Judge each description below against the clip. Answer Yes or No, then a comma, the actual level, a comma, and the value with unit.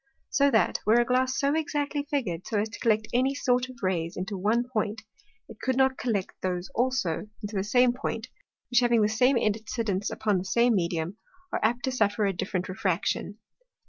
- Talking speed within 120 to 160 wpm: No, average, 200 wpm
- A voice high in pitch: Yes, high, 225 Hz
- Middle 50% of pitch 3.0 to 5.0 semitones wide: Yes, average, 4.3 semitones